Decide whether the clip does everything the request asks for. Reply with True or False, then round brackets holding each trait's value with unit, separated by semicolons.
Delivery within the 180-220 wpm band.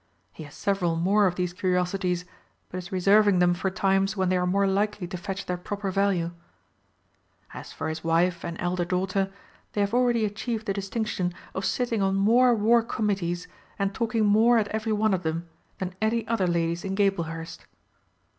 True (185 wpm)